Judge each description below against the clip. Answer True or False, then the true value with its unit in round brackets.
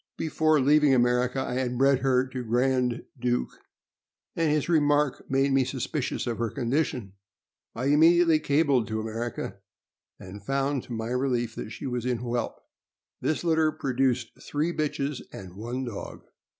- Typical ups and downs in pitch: True (3.3 semitones)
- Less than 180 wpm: True (150 wpm)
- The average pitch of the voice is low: True (130 Hz)